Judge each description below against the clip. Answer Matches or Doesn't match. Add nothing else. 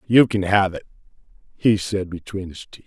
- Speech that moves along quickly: Doesn't match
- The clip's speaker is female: Doesn't match